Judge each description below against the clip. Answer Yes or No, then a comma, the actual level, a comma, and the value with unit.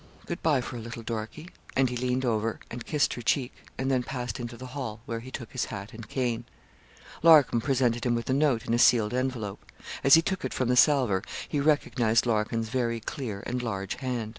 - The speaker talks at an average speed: No, fast, 220 wpm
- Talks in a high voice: No, low, 120 Hz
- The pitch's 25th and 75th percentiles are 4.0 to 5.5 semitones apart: No, narrow, 2.4 semitones